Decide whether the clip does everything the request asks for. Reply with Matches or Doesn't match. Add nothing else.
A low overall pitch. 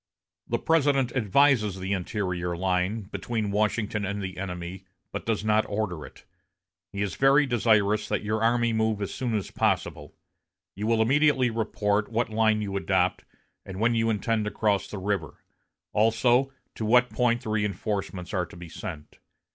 Matches